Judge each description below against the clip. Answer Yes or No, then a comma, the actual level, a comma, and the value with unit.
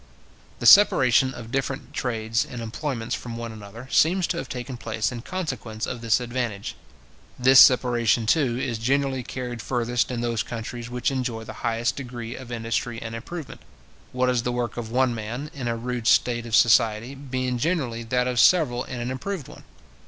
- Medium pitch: No, low, 120 Hz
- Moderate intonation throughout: No, narrow, 2.0 semitones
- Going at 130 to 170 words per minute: No, average, 180 wpm